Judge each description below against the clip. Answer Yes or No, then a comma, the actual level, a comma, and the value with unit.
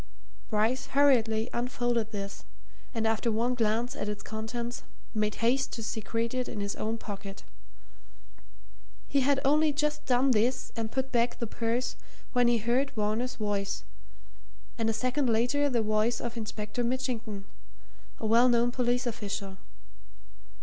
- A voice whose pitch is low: No, high, 235 Hz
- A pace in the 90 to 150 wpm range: Yes, average, 145 wpm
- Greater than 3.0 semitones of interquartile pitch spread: No, narrow, 2.4 semitones